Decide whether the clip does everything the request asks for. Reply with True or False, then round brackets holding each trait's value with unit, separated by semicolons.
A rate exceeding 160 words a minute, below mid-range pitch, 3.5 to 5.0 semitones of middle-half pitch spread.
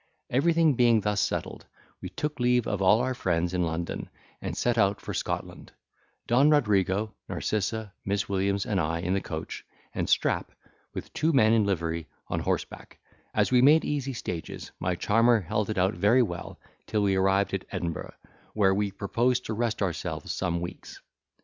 True (175 wpm; 105 Hz; 4.4 semitones)